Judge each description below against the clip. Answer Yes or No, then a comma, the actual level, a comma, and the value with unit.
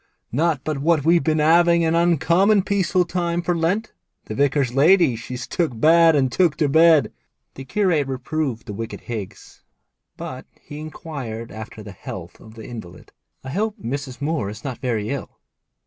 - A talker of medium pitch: Yes, medium, 150 Hz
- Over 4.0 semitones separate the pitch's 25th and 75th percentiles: Yes, wide, 5.6 semitones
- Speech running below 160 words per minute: No, average, 170 wpm